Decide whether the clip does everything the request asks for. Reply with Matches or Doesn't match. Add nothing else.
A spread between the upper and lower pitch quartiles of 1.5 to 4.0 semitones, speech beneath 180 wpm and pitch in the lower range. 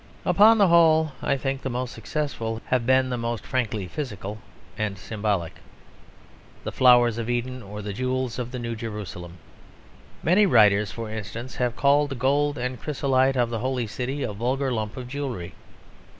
Matches